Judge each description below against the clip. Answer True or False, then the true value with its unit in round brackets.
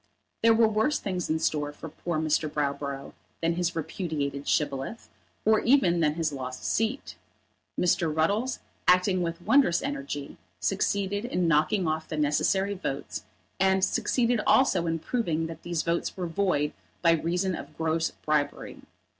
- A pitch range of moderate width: True (4.4 semitones)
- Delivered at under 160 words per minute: True (150 wpm)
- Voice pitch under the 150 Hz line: False (170 Hz)